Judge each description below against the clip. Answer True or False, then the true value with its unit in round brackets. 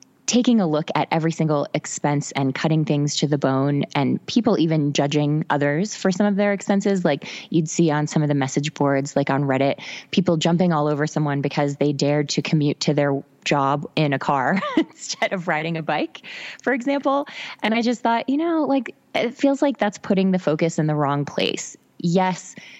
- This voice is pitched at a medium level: True (160 Hz)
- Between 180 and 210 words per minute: True (205 wpm)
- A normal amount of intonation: False (6.1 semitones)